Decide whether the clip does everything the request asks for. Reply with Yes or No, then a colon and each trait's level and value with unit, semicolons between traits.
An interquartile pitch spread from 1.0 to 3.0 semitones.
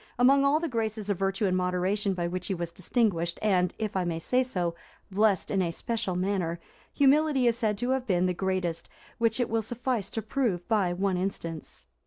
No: average, 4.3 semitones